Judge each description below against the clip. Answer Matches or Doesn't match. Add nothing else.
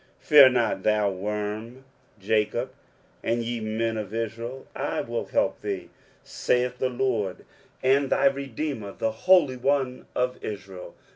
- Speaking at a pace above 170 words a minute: Doesn't match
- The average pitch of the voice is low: Matches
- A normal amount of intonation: Matches